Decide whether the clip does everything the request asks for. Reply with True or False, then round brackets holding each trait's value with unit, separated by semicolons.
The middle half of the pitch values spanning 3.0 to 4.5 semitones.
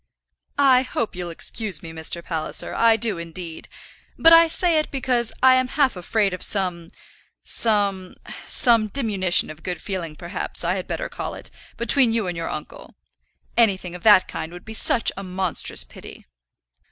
False (5.0 semitones)